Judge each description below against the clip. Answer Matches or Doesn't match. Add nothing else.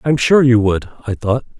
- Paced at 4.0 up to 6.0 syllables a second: Matches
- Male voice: Matches